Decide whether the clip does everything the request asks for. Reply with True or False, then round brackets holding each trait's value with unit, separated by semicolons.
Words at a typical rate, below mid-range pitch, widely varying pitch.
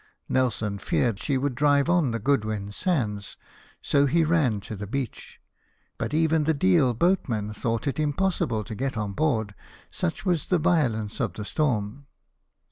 True (155 wpm; 130 Hz; 6.1 semitones)